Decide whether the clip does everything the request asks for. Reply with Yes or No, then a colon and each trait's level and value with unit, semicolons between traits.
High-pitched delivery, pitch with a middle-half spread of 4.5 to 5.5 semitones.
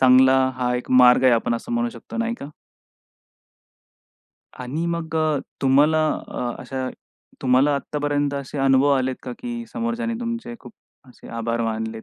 No: low, 135 Hz; average, 4.9 semitones